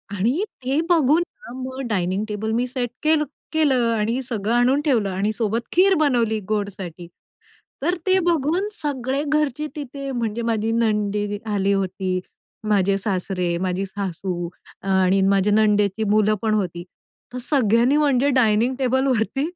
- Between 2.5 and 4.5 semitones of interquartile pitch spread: No, average, 5.1 semitones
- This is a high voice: Yes, high, 225 Hz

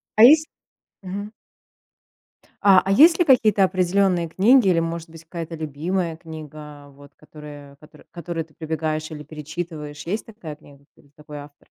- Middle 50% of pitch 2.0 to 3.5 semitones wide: No, average, 4.0 semitones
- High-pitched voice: No, medium, 165 Hz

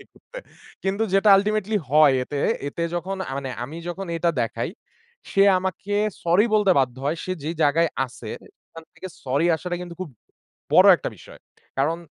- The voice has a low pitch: No, medium, 170 Hz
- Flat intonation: No, average, 5.2 semitones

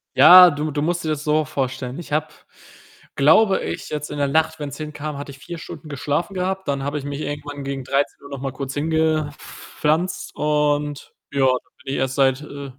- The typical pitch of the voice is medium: Yes, medium, 145 Hz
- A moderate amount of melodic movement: No, narrow, 1.9 semitones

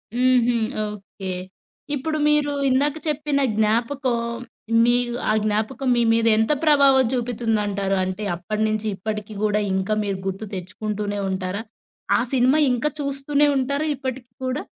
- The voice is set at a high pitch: Yes, high, 235 Hz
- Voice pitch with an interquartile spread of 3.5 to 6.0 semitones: Yes, average, 4.6 semitones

